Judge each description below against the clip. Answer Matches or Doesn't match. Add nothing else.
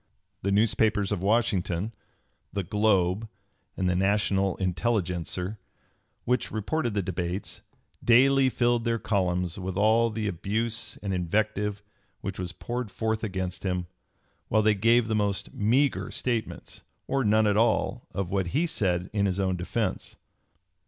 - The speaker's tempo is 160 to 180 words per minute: Doesn't match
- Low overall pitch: Matches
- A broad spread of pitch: Doesn't match